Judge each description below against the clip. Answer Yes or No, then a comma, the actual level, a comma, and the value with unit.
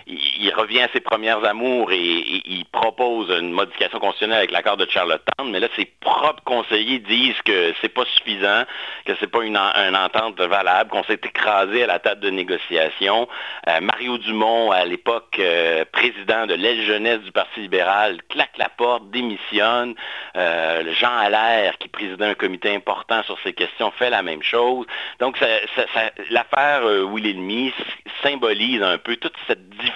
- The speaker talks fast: No, average, 180 wpm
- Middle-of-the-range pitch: No, low, 110 Hz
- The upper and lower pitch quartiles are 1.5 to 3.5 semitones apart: No, average, 4.1 semitones